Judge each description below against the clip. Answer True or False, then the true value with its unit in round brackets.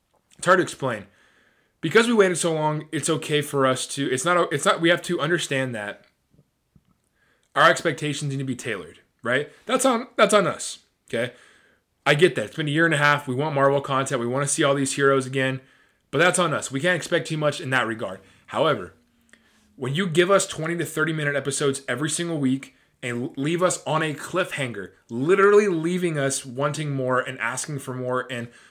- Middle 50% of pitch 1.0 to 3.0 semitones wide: False (4.2 semitones)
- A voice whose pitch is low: False (145 Hz)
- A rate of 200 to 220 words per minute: True (205 wpm)